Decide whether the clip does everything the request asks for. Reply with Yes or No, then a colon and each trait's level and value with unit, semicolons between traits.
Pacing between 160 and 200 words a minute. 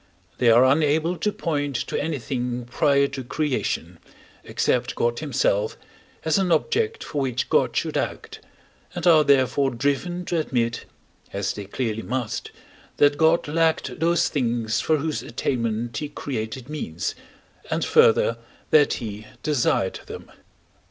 No: average, 140 wpm